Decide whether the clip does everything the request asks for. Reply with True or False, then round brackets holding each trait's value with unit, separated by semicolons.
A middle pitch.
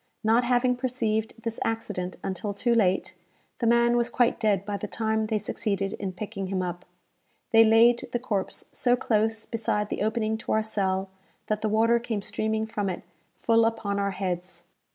False (220 Hz)